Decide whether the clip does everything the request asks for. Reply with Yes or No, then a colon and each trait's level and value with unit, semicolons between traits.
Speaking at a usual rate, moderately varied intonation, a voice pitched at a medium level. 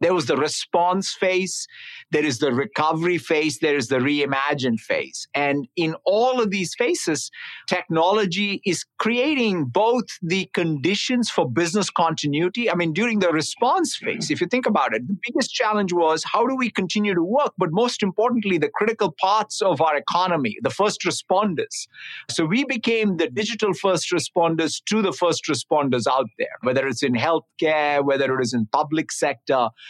No: average, 175 wpm; wide, 5.7 semitones; medium, 180 Hz